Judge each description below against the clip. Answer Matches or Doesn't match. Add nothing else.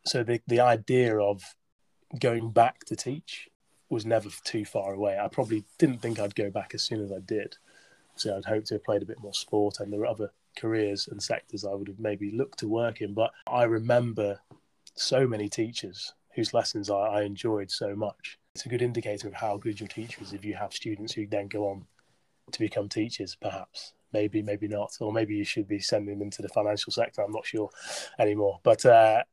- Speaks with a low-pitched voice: Matches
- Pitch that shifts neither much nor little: Doesn't match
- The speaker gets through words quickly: Matches